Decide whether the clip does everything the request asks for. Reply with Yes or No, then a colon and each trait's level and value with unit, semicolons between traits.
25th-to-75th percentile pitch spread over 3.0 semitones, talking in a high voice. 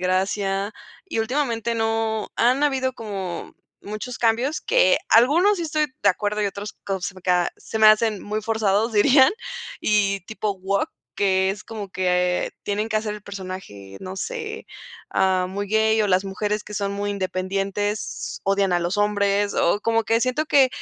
No: narrow, 2.6 semitones; high, 205 Hz